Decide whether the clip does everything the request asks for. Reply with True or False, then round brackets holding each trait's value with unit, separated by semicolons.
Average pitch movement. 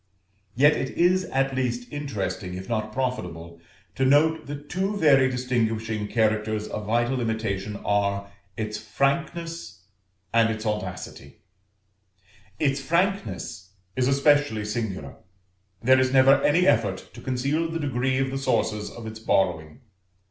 True (4.6 semitones)